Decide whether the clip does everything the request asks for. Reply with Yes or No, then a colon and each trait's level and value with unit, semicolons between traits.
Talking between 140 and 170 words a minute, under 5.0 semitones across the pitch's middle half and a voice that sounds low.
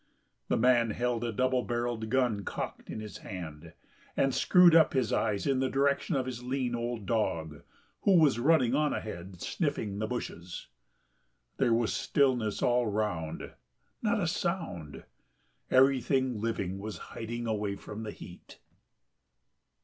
Yes: average, 145 wpm; average, 4.0 semitones; low, 120 Hz